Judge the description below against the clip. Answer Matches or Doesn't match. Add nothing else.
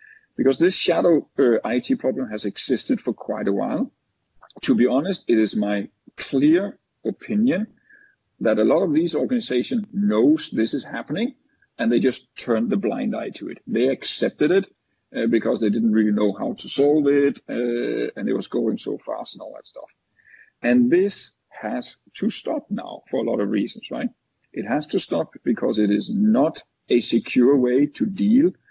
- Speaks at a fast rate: Doesn't match